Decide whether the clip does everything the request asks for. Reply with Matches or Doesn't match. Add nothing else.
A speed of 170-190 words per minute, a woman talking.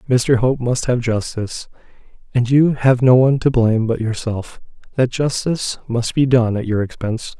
Doesn't match